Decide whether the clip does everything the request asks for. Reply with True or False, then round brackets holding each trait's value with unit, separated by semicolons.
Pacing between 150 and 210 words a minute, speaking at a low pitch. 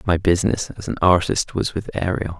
True (200 wpm; 90 Hz)